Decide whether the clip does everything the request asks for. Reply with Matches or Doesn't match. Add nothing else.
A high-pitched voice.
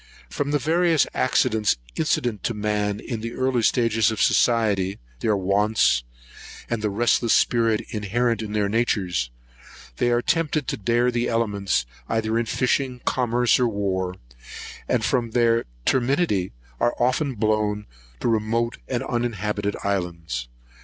Doesn't match